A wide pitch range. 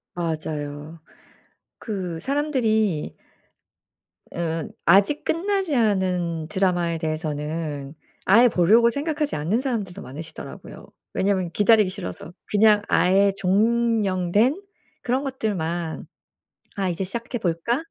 Yes: wide, 5.7 semitones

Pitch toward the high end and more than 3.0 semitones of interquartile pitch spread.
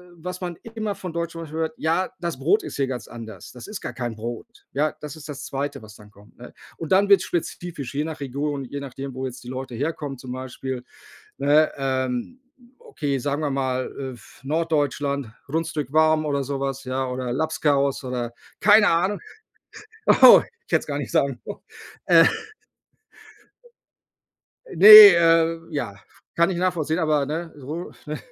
No: medium, 145 Hz; average, 4.0 semitones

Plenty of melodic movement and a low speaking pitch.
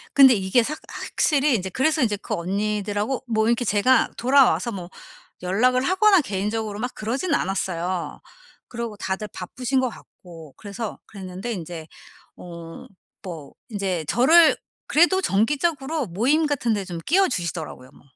No: wide, 6.0 semitones; high, 220 Hz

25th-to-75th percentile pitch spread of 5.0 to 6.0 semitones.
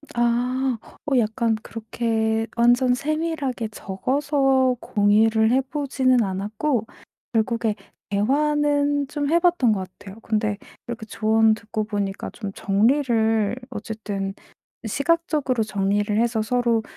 No: average, 3.7 semitones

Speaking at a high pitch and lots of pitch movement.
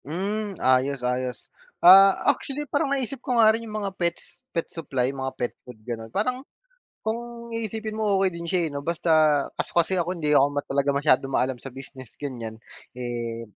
No: medium, 165 Hz; wide, 8.6 semitones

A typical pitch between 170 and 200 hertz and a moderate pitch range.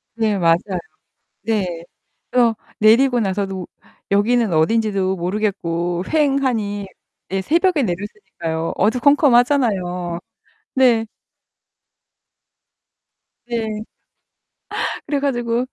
No: high, 215 Hz; average, 4.6 semitones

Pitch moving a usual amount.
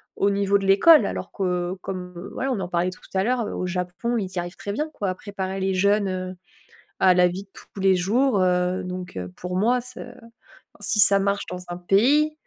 No: narrow, 2.3 semitones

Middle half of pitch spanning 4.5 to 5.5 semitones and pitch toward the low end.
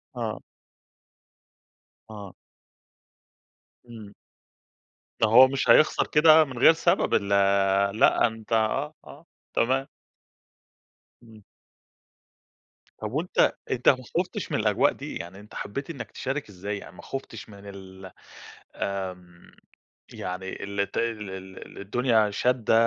Yes: average, 4.9 semitones; low, 110 Hz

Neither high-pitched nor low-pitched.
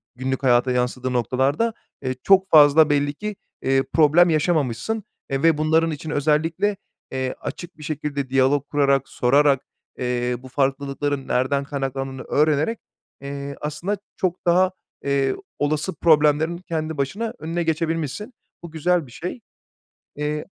Yes: medium, 145 Hz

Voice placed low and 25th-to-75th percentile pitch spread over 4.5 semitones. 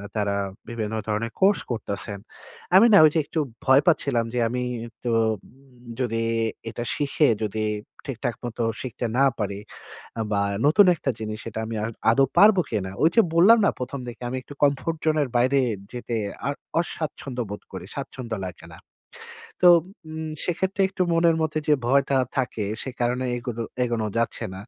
Yes: low, 125 Hz; wide, 5.4 semitones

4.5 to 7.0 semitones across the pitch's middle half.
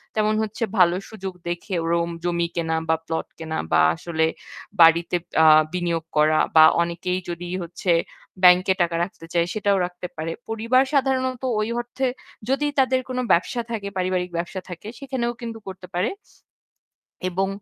Yes: average, 4.8 semitones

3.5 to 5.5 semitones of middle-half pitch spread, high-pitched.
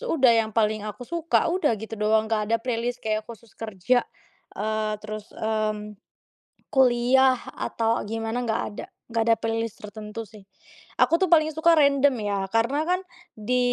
No: average, 2.8 semitones; high, 225 Hz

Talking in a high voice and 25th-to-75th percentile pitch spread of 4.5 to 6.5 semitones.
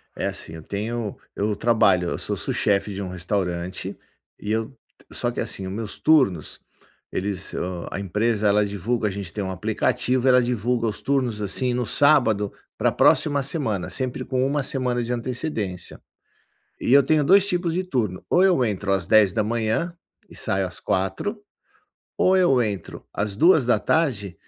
No: low, 110 Hz; average, 5.0 semitones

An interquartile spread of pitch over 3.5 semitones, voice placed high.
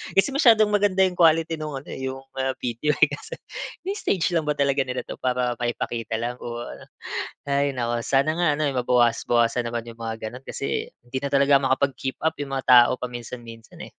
No: average, 3.9 semitones; low, 130 Hz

